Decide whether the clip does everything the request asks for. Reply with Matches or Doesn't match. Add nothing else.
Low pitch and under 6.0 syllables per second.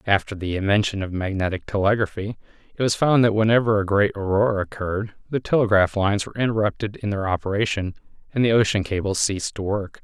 Doesn't match